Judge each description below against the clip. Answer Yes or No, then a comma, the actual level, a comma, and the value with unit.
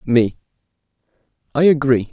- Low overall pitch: Yes, low, 125 Hz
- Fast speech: No, slow, 85 wpm